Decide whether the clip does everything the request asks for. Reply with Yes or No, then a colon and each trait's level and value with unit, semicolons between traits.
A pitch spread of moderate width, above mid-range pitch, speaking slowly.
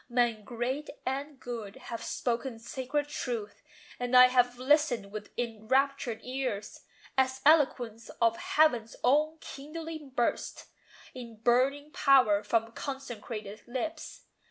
Yes: average, 3.2 semitones; very high, 250 Hz; slow, 115 wpm